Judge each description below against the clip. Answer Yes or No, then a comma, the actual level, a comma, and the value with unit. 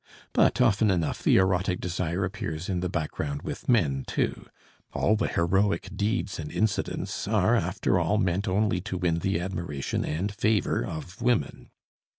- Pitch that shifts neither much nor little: Yes, average, 3.5 semitones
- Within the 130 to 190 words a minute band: Yes, average, 160 wpm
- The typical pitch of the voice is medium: No, very low, 95 Hz